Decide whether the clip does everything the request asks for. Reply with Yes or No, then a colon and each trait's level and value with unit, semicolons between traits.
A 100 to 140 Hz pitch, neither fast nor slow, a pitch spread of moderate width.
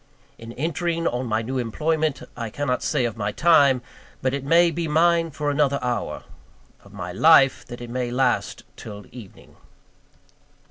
Yes: low, 135 Hz; average, 160 wpm; average, 4.7 semitones